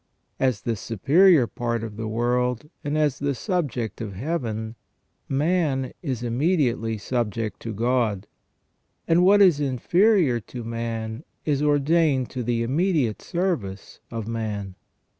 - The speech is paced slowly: Yes, slow, 130 wpm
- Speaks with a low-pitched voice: Yes, low, 125 Hz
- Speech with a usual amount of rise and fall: Yes, average, 4.9 semitones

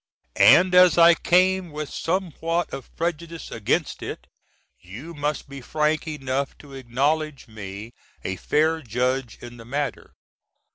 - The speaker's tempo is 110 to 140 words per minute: Yes, slow, 135 wpm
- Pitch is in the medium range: Yes, medium, 150 Hz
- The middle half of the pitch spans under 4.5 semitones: No, average, 4.8 semitones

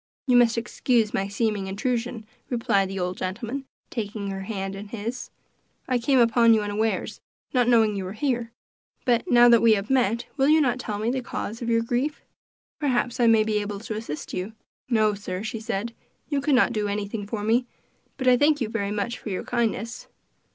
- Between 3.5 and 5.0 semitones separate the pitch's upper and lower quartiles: No, average, 2.9 semitones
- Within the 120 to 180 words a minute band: No, average, 200 wpm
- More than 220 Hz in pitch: Yes, high, 230 Hz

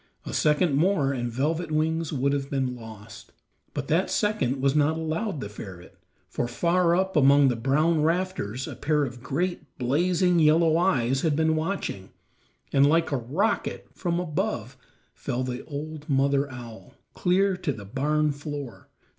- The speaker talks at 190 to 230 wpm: No, average, 160 wpm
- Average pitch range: Yes, average, 4.2 semitones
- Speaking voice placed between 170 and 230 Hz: No, medium, 145 Hz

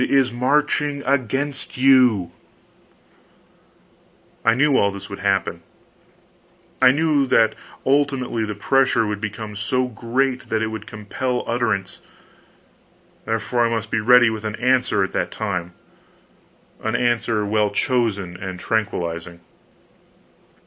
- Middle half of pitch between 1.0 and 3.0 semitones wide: No, average, 3.8 semitones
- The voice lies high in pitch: No, low, 115 Hz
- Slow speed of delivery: Yes, slow, 120 wpm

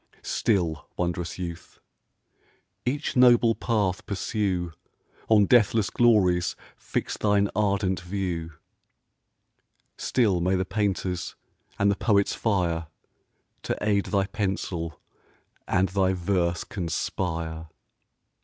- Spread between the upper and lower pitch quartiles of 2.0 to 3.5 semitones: Yes, average, 2.9 semitones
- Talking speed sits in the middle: No, slow, 100 wpm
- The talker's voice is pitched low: Yes, very low, 95 Hz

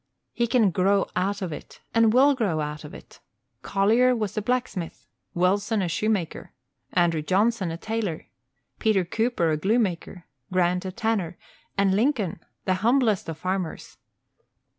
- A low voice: No, high, 195 Hz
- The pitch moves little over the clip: No, average, 4.2 semitones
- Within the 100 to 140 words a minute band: No, average, 150 wpm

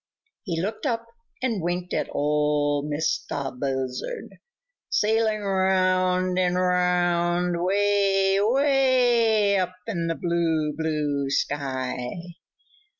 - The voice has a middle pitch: Yes, medium, 180 Hz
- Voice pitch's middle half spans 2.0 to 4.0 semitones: No, average, 5.1 semitones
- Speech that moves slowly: Yes, slow, 95 wpm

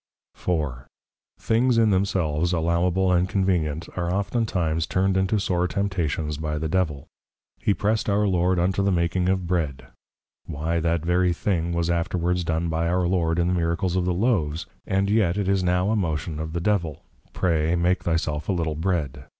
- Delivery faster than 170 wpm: Yes, average, 185 wpm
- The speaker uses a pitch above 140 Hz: No, very low, 85 Hz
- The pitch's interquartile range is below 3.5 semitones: Yes, narrow, 2.6 semitones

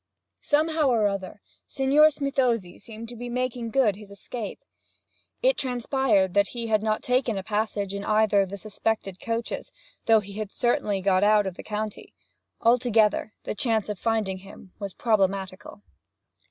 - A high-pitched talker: Yes, high, 215 Hz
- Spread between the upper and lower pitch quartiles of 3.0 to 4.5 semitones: Yes, average, 3.3 semitones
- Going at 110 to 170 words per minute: Yes, average, 160 wpm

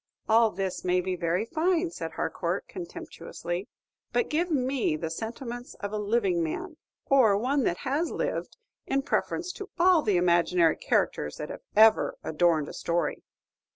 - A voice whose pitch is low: No, high, 220 Hz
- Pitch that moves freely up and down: Yes, wide, 8.2 semitones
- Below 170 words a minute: Yes, average, 155 wpm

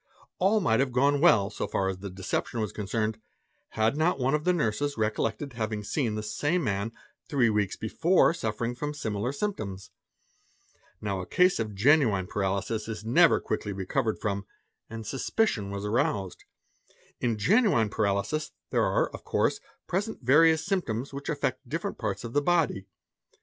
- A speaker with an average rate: Yes, average, 175 wpm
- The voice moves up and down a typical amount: No, wide, 6.0 semitones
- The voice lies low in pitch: Yes, low, 115 Hz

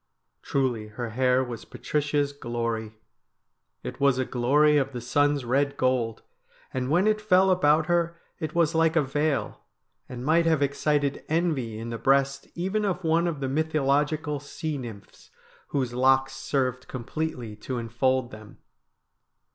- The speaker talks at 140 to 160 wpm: Yes, average, 155 wpm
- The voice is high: No, medium, 140 Hz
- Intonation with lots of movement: No, average, 3.7 semitones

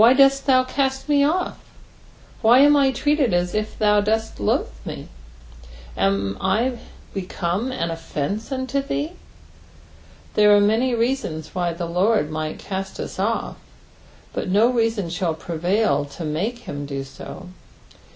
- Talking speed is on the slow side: No, average, 150 wpm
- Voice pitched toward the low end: No, high, 210 Hz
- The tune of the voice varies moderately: No, wide, 7.2 semitones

